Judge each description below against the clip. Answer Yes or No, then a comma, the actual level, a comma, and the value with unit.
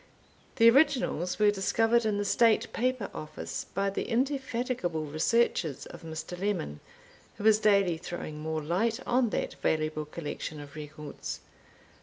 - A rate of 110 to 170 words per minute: Yes, average, 140 wpm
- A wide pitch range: Yes, wide, 6.8 semitones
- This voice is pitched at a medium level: No, high, 195 Hz